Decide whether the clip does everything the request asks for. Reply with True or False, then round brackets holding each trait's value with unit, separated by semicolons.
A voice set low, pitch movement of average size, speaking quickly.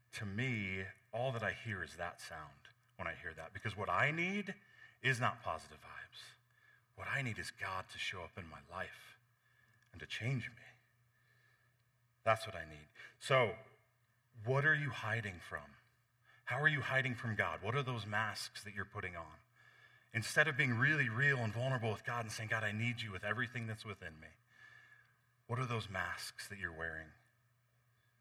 False (115 Hz; 3.1 semitones; 185 wpm)